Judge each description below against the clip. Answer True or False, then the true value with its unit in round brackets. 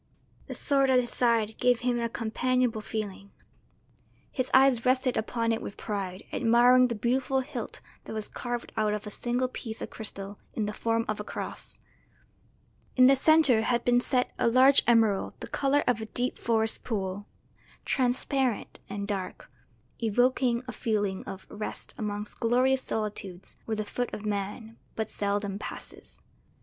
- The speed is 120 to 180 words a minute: True (160 wpm)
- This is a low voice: False (230 Hz)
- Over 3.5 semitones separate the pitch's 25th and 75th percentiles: False (3.1 semitones)